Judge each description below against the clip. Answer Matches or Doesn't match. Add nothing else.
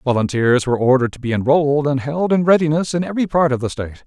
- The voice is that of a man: Matches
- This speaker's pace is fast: Matches